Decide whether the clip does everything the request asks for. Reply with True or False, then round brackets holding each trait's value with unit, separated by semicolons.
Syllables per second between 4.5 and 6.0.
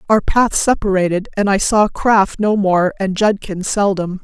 False (4.3 syllables/s)